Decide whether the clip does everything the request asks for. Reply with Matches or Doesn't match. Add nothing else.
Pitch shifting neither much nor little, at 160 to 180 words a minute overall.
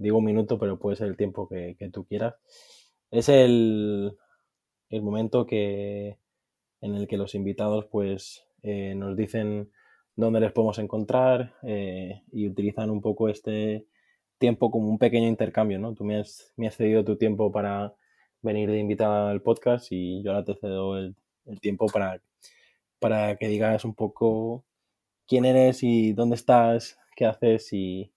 Doesn't match